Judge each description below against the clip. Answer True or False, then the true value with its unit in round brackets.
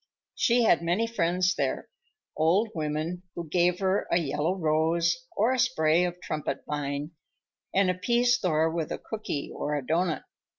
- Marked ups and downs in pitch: False (3.4 semitones)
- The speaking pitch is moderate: True (170 Hz)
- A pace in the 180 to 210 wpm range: False (160 wpm)